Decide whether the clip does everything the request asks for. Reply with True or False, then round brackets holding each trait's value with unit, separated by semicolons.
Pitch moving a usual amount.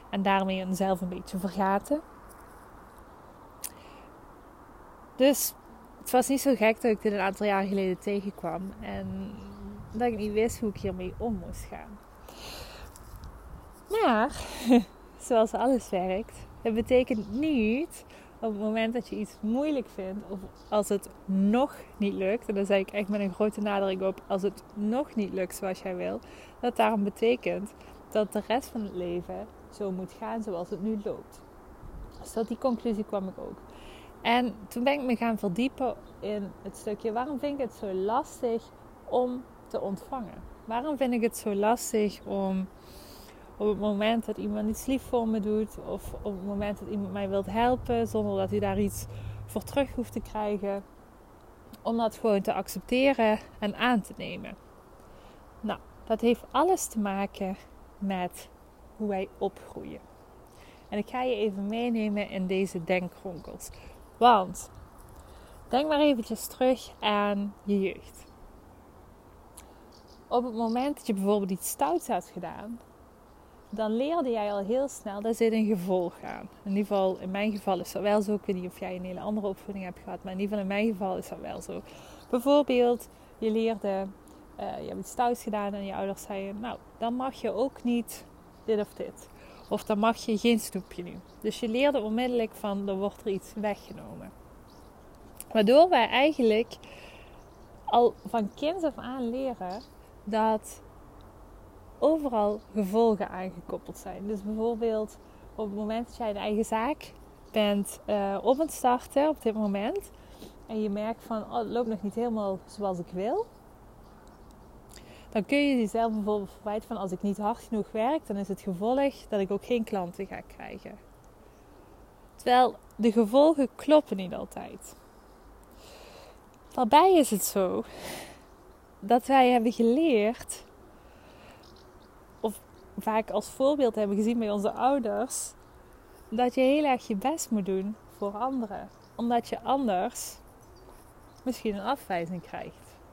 True (3.3 semitones)